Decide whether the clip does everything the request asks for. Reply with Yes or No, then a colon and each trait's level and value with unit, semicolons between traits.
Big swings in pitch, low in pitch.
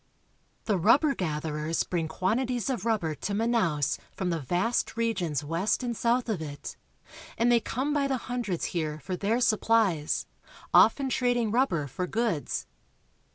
No: wide, 6.5 semitones; high, 210 Hz